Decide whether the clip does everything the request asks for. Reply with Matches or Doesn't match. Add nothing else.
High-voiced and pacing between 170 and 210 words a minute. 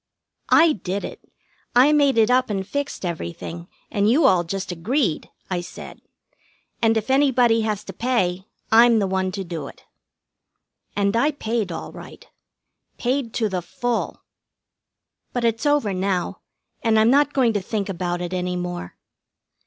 Doesn't match